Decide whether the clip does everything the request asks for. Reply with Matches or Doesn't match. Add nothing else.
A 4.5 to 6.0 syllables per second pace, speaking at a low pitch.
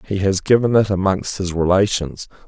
Matches